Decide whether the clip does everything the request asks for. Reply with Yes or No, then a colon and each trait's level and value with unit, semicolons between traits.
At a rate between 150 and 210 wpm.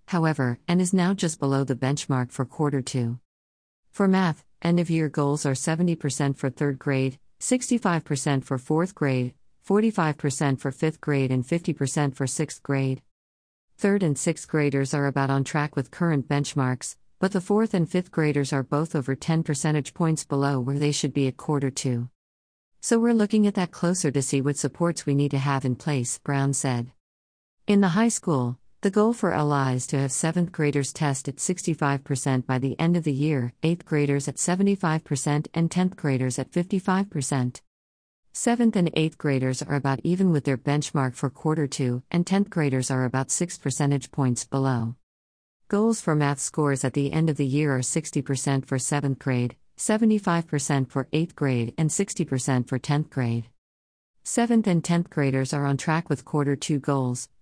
Yes: average, 180 wpm